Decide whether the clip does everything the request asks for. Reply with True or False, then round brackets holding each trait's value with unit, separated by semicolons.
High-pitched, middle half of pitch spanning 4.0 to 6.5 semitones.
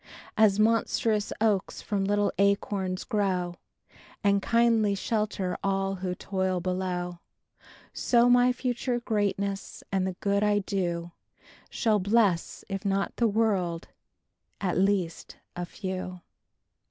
False (200 Hz; 2.4 semitones)